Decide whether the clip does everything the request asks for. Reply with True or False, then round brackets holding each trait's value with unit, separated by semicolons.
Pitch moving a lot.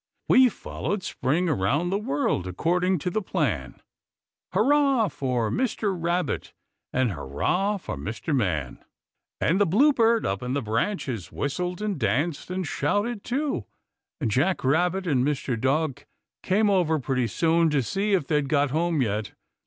True (6.9 semitones)